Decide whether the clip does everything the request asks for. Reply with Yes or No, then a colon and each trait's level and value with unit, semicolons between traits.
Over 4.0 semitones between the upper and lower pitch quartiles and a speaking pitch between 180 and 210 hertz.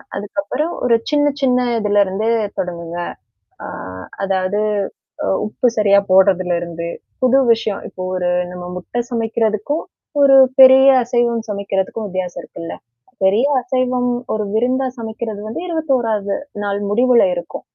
No: average, 4.6 semitones; high, 220 Hz